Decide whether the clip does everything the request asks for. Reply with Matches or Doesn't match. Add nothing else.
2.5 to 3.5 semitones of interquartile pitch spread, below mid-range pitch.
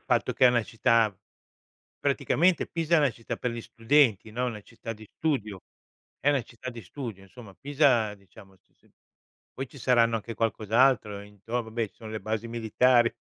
Matches